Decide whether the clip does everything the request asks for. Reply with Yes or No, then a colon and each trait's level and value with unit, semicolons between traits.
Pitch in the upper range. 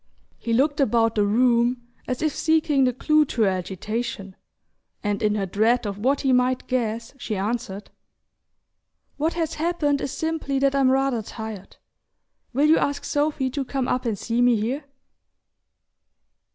Yes: very high, 250 Hz